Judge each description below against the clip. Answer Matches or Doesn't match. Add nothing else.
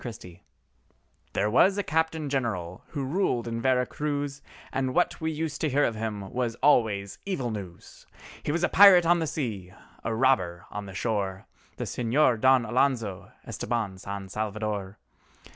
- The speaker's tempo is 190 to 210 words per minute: Doesn't match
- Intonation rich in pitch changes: Matches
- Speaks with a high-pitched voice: Doesn't match